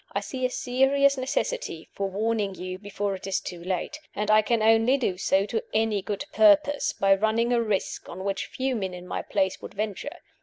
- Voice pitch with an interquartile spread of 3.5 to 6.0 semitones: Yes, average, 4.7 semitones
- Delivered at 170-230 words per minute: Yes, fast, 205 wpm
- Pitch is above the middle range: Yes, high, 215 Hz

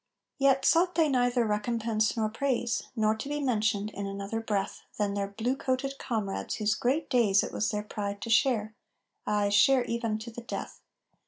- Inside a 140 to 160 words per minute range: No, average, 185 wpm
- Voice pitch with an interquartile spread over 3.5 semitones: No, average, 3.2 semitones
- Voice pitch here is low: No, high, 225 Hz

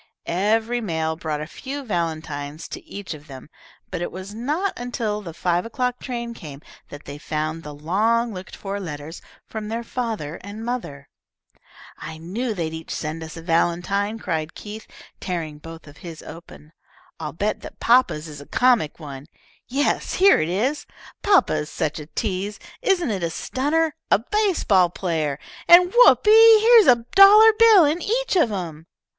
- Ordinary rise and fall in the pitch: No, wide, 7.7 semitones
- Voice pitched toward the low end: No, high, 195 Hz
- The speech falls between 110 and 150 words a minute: No, average, 170 wpm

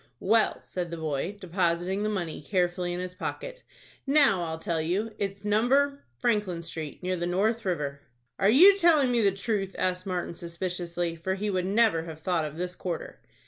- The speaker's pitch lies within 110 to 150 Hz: No, medium, 185 Hz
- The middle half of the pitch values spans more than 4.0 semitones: No, average, 3.6 semitones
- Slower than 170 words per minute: No, average, 185 wpm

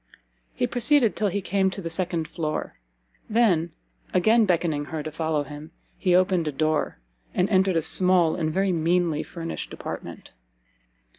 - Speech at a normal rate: Yes, average, 155 wpm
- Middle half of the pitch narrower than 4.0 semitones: Yes, average, 3.2 semitones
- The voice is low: No, medium, 175 Hz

